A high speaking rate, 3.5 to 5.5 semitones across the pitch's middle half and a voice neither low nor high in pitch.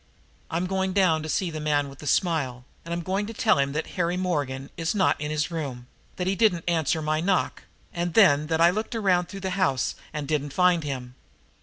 Yes: fast, 220 wpm; average, 3.9 semitones; medium, 165 Hz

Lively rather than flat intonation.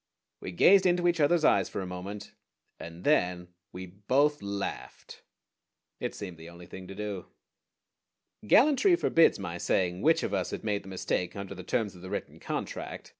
Yes: wide, 8.3 semitones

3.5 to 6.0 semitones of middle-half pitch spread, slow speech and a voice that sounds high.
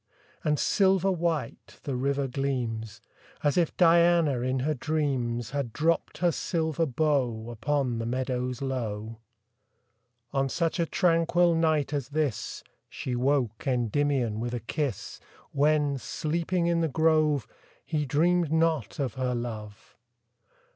No: average, 4.6 semitones; slow, 130 wpm; medium, 140 Hz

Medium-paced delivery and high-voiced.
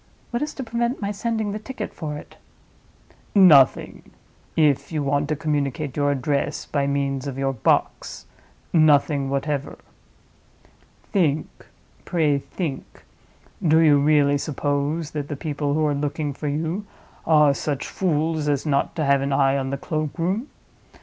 No: average, 145 wpm; medium, 150 Hz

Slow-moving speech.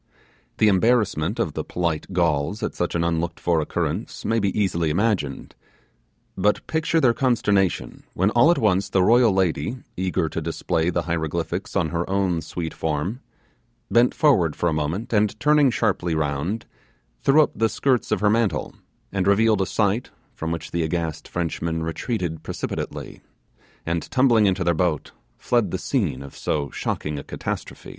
No: average, 165 wpm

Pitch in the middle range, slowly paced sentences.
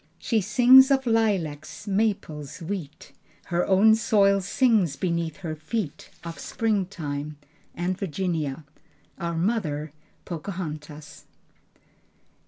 Yes: medium, 180 Hz; slow, 95 wpm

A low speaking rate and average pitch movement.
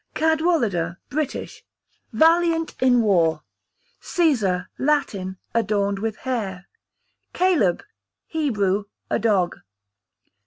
No: slow, 80 wpm; wide, 8.4 semitones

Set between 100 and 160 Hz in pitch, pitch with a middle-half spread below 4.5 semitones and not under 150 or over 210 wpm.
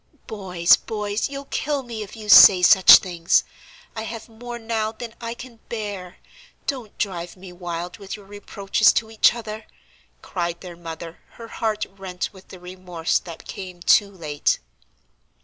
No: high, 200 Hz; average, 3.8 semitones; average, 160 wpm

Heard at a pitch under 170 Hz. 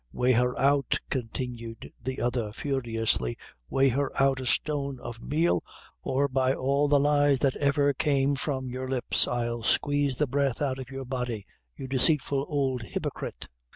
Yes: low, 135 Hz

